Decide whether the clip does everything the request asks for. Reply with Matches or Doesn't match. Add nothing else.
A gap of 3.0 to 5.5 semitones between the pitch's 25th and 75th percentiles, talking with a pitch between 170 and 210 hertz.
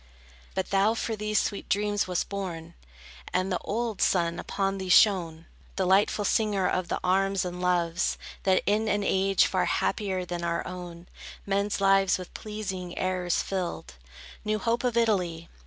Doesn't match